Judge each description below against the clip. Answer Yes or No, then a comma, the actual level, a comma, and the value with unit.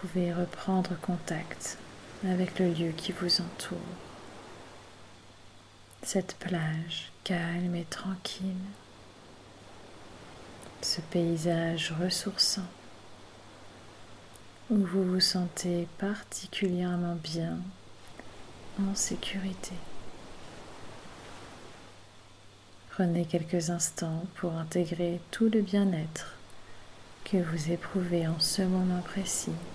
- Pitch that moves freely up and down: Yes, wide, 8.9 semitones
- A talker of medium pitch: Yes, medium, 170 Hz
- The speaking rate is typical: No, slow, 85 wpm